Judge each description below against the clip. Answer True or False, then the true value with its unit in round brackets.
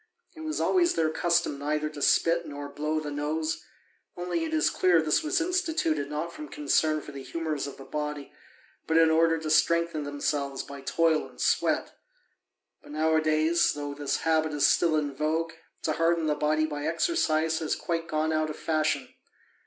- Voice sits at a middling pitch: True (155 Hz)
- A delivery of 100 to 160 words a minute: False (180 wpm)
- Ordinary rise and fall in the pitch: False (1.9 semitones)